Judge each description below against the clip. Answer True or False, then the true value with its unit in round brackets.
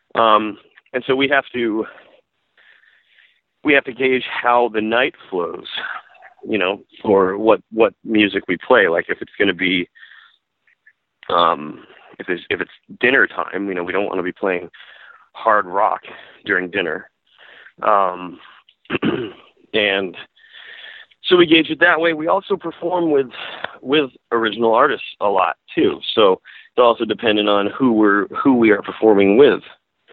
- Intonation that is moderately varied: False (8.3 semitones)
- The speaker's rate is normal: True (155 wpm)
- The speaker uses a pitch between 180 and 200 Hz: False (120 Hz)